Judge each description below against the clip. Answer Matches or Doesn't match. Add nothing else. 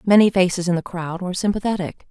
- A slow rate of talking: Doesn't match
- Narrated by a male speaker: Doesn't match